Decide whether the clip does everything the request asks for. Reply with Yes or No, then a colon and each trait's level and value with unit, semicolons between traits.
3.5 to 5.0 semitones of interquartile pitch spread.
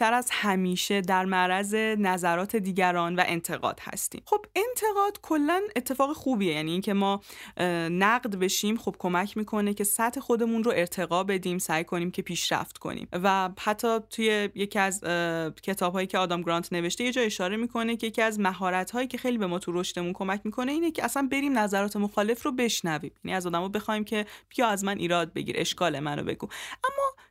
Yes: average, 4.4 semitones